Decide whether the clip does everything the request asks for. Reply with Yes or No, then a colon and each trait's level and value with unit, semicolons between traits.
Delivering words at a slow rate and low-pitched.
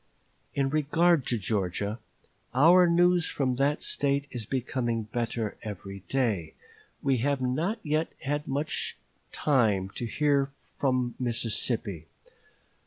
Yes: slow, 115 wpm; low, 130 Hz